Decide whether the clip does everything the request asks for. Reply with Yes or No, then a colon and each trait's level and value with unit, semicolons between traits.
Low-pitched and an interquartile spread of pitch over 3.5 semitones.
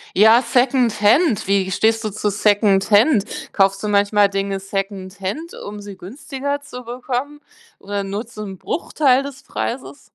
No: high, 210 Hz; average, 4.2 semitones